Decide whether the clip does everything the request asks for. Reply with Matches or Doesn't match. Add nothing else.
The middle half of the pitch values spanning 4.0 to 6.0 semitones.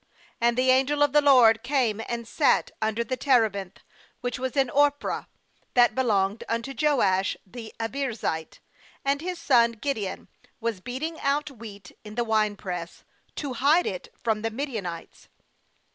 Matches